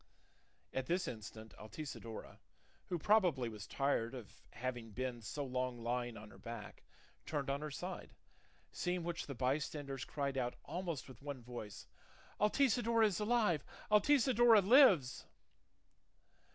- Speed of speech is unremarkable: No, slow, 130 wpm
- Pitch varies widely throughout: Yes, wide, 7.0 semitones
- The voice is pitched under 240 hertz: Yes, medium, 140 Hz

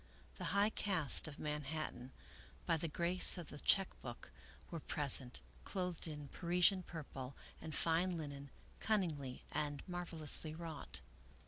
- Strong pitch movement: No, average, 3.6 semitones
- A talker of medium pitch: Yes, medium, 160 Hz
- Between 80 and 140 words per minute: Yes, slow, 135 wpm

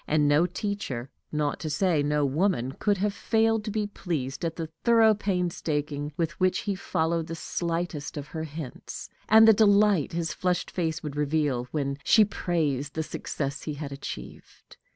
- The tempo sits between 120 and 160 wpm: No, average, 170 wpm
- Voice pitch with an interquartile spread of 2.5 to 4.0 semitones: No, average, 5.0 semitones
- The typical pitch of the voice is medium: Yes, medium, 160 Hz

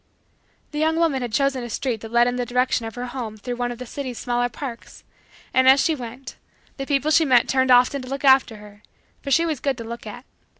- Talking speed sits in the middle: No, fast, 245 wpm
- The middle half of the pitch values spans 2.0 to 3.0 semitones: Yes, narrow, 2.4 semitones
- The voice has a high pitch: Yes, very high, 250 Hz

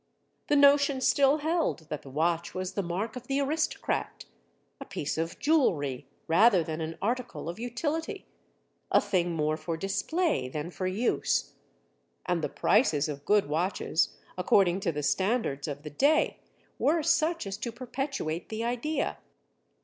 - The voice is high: Yes, high, 195 Hz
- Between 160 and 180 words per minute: No, average, 150 wpm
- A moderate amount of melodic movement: No, wide, 9.0 semitones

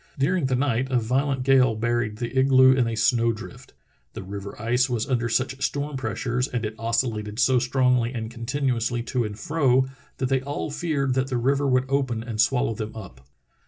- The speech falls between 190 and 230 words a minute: Yes, average, 195 wpm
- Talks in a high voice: No, low, 125 Hz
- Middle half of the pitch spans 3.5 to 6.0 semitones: No, narrow, 2.6 semitones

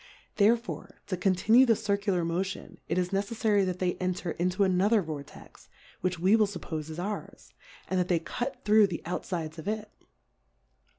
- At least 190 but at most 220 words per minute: No, average, 170 wpm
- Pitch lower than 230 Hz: Yes, medium, 185 Hz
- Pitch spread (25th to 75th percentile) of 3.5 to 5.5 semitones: No, average, 2.9 semitones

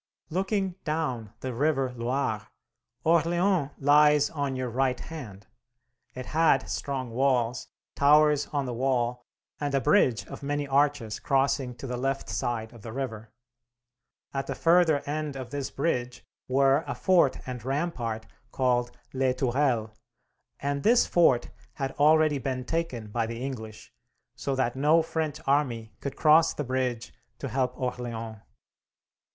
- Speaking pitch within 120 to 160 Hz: Yes, low, 135 Hz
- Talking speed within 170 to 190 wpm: No, average, 145 wpm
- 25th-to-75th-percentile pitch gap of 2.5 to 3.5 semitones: Yes, average, 3.2 semitones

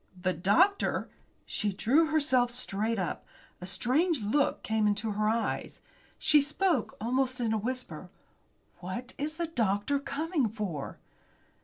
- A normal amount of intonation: No, wide, 5.7 semitones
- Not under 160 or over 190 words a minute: No, slow, 135 wpm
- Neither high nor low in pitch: No, high, 240 Hz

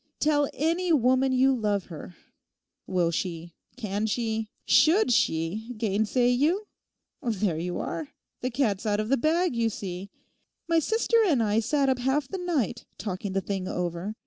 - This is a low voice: No, high, 230 Hz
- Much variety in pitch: Yes, wide, 6.0 semitones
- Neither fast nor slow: Yes, average, 160 wpm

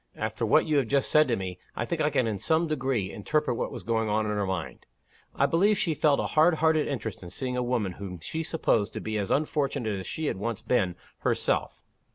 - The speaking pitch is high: No, low, 125 Hz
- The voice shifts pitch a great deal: Yes, wide, 6.8 semitones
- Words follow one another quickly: Yes, fast, 235 wpm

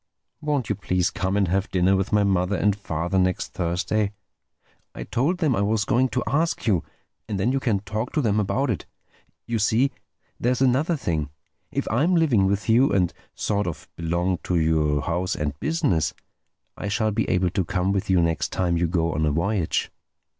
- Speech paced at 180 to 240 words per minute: Yes, average, 190 wpm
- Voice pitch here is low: Yes, low, 100 Hz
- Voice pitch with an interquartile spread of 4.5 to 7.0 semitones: Yes, average, 4.8 semitones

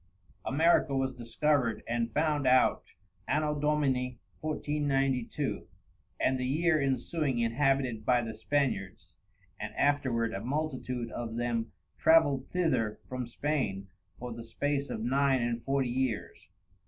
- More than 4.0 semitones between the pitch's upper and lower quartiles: No, average, 3.5 semitones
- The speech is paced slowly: Yes, slow, 125 wpm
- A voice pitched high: No, low, 130 Hz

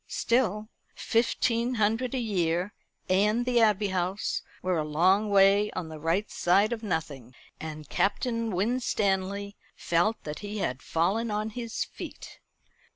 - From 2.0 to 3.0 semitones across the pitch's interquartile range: No, average, 4.1 semitones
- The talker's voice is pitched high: Yes, high, 205 Hz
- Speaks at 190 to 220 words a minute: No, average, 140 wpm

